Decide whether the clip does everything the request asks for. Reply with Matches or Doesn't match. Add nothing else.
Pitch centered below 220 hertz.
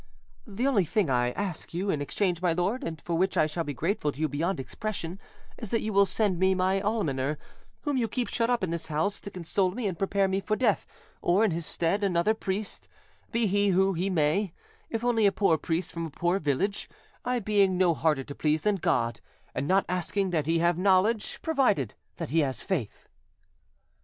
Matches